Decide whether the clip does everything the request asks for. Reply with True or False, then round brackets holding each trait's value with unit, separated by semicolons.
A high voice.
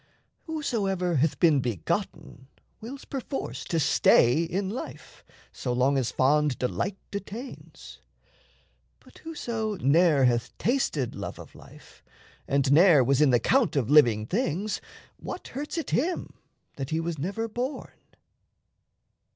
False (165 Hz)